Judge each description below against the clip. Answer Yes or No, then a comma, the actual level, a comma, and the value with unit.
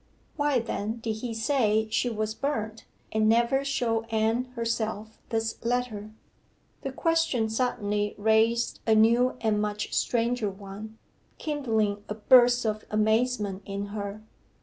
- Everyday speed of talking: No, slow, 130 wpm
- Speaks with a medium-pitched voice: No, high, 220 Hz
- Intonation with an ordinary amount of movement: No, narrow, 2.3 semitones